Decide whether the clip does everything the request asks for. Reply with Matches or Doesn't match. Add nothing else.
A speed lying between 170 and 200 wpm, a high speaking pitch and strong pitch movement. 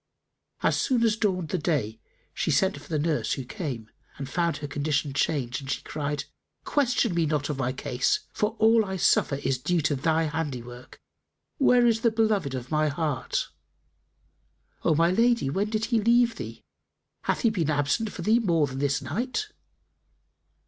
Doesn't match